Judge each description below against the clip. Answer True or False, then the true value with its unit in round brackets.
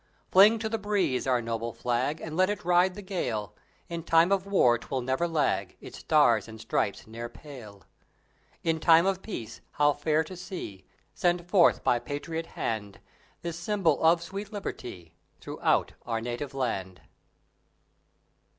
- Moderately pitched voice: True (155 Hz)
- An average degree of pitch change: False (7.1 semitones)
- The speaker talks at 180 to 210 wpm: False (155 wpm)